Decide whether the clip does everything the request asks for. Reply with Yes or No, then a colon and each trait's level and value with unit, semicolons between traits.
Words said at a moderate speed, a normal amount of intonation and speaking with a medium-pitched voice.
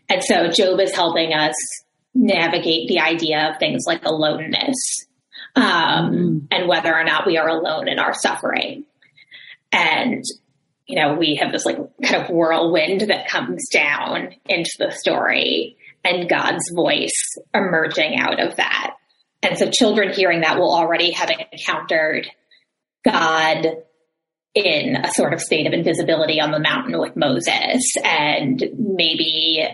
Yes: average, 145 wpm; average, 3.4 semitones; medium, 170 Hz